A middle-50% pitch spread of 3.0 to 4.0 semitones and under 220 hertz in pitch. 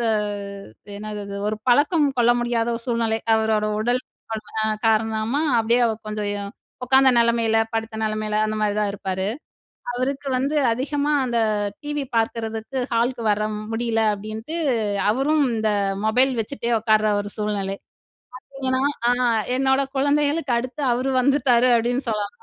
No: average, 3.4 semitones; high, 230 Hz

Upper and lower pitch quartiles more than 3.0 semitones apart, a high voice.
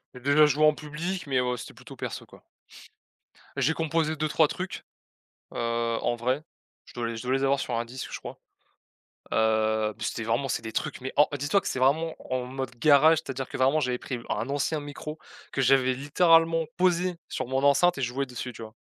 No: average, 3.7 semitones; low, 135 Hz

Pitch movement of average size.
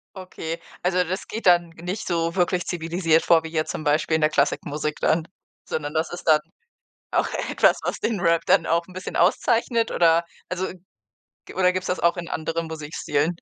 No: narrow, 2.2 semitones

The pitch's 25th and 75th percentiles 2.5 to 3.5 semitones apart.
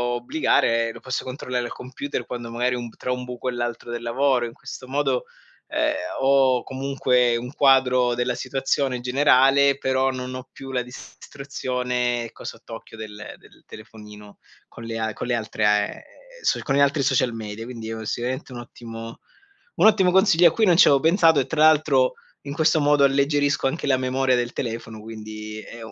Yes: average, 2.8 semitones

